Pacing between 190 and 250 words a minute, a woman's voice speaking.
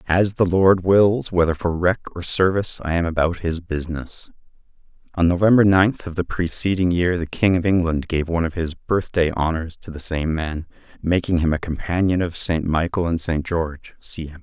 No: average, 200 wpm; male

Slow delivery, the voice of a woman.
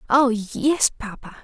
Yes: slow, 125 wpm; female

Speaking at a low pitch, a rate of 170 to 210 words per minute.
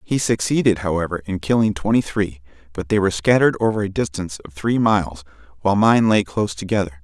Yes: low, 100 Hz; average, 190 wpm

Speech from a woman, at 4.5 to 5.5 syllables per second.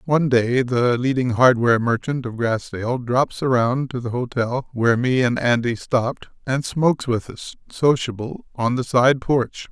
No: male; 4.6 syllables/s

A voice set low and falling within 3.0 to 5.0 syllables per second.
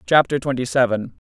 No: low, 130 Hz; 5.2 syllables/s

